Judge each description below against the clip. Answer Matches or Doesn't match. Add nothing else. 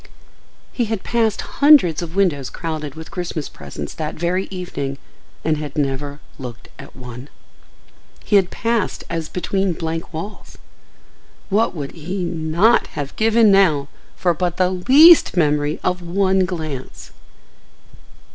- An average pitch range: Matches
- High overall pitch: Doesn't match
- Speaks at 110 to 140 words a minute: Matches